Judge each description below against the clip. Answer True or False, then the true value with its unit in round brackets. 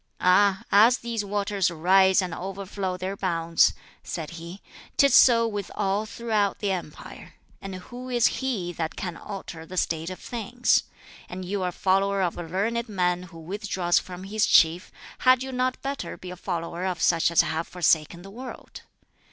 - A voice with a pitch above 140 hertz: True (190 Hz)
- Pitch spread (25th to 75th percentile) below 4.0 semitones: True (3.2 semitones)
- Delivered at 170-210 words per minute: True (175 wpm)